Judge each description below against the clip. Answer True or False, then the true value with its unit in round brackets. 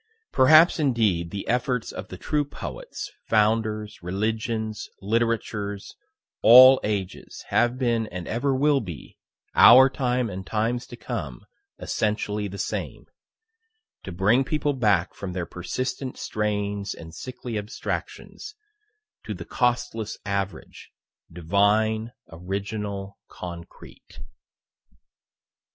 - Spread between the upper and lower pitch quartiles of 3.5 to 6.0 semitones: True (3.9 semitones)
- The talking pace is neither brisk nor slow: False (105 wpm)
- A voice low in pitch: True (110 Hz)